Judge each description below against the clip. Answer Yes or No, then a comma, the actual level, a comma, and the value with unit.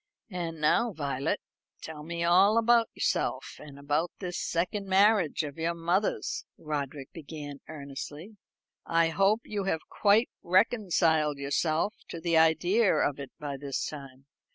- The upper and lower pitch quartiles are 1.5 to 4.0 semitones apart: No, average, 4.7 semitones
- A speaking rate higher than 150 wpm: No, average, 140 wpm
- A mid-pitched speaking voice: Yes, medium, 165 Hz